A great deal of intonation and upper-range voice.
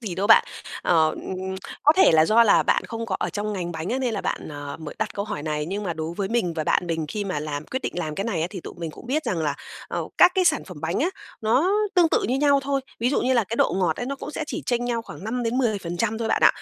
Yes: wide, 6.6 semitones; high, 210 Hz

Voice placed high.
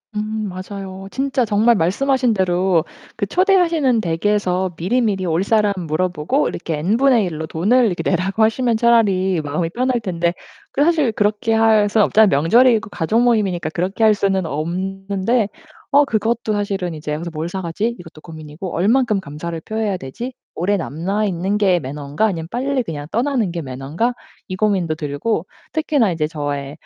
Yes: high, 195 Hz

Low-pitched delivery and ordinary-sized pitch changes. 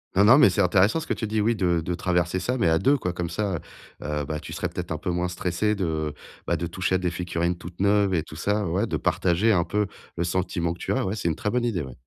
Yes: very low, 90 Hz; average, 3.3 semitones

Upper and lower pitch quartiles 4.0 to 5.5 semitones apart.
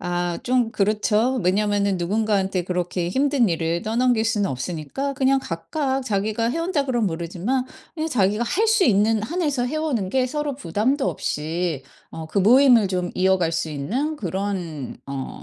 No: wide, 6.7 semitones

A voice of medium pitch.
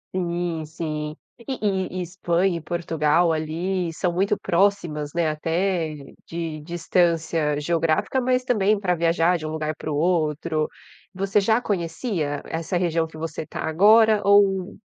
Yes: medium, 170 Hz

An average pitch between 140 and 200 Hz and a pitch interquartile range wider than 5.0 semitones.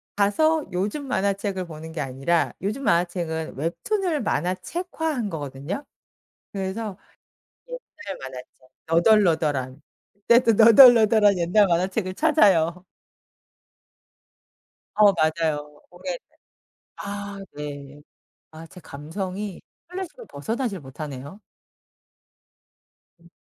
Yes: high, 190 Hz; wide, 5.5 semitones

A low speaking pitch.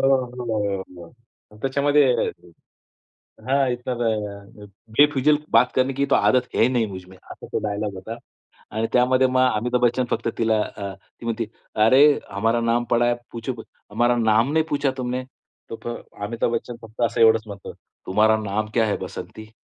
Yes: low, 115 Hz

